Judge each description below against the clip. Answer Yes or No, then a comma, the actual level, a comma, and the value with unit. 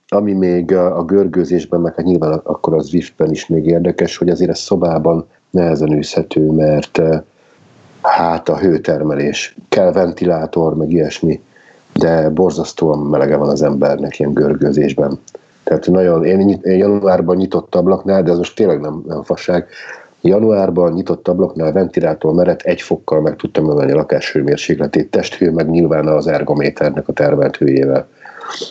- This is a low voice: Yes, very low, 85 Hz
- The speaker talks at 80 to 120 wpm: No, average, 140 wpm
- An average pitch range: No, narrow, 2.3 semitones